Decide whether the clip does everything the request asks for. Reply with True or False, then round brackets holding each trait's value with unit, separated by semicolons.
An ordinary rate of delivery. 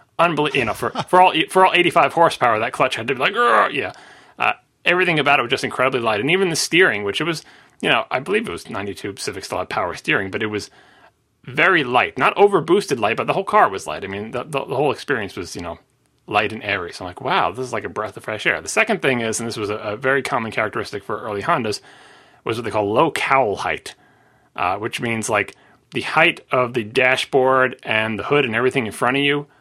False (250 wpm)